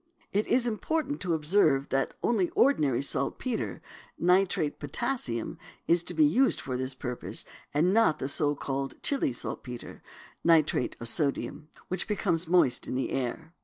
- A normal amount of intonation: No, wide, 7.1 semitones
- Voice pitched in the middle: Yes, medium, 160 Hz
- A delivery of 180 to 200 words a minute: No, average, 155 wpm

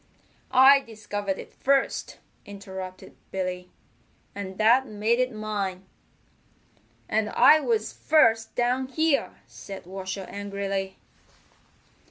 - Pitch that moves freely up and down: No, average, 4.3 semitones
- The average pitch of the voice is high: Yes, high, 210 Hz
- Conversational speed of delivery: No, slow, 100 wpm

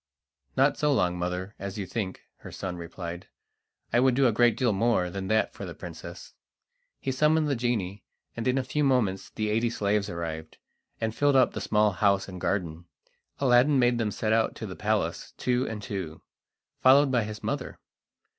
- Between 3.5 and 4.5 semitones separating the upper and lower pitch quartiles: No, average, 5.1 semitones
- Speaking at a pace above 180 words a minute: Yes, average, 190 wpm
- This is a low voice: Yes, low, 110 Hz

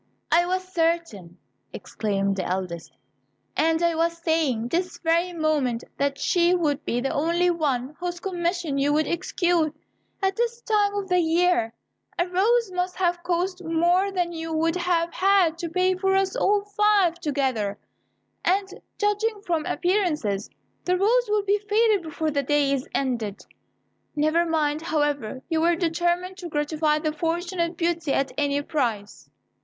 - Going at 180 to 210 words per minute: No, average, 155 wpm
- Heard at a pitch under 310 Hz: No, very high, 335 Hz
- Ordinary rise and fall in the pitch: Yes, average, 3.8 semitones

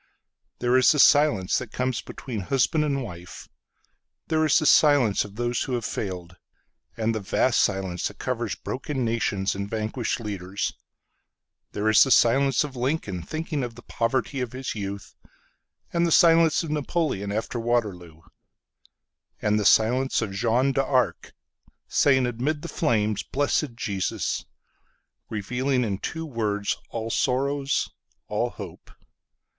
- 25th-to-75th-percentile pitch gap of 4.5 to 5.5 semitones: Yes, average, 4.8 semitones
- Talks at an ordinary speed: No, slow, 120 wpm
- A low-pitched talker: Yes, low, 120 Hz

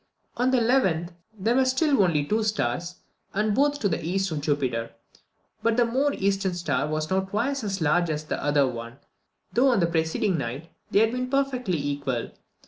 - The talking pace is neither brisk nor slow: Yes, average, 190 wpm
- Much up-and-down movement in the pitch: Yes, wide, 7.5 semitones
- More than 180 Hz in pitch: Yes, high, 190 Hz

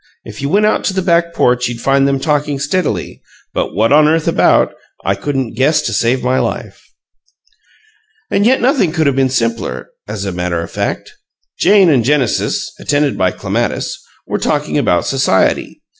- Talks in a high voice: No, medium, 140 Hz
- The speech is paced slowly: No, average, 175 wpm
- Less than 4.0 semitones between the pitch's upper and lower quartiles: No, wide, 5.5 semitones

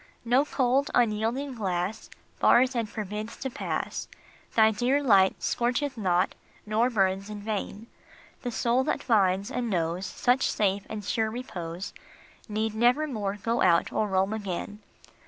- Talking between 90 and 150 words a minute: Yes, average, 140 wpm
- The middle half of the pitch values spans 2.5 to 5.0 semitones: Yes, average, 3.7 semitones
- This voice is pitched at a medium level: No, high, 220 Hz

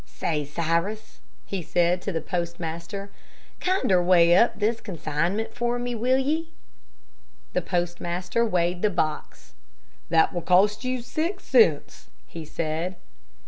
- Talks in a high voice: No, medium, 180 Hz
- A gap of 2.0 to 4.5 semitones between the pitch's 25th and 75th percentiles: No, average, 5.1 semitones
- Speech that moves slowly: Yes, slow, 130 wpm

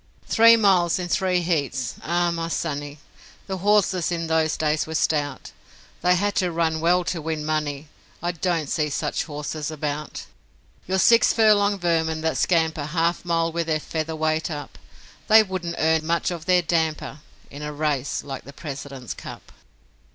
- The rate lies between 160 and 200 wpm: Yes, average, 170 wpm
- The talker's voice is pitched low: No, medium, 160 Hz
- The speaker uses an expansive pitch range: No, narrow, 2.6 semitones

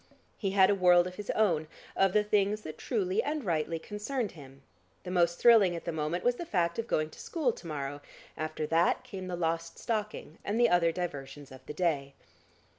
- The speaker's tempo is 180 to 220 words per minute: Yes, fast, 205 wpm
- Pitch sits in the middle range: Yes, medium, 180 Hz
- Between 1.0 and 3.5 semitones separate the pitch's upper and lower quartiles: No, average, 4.9 semitones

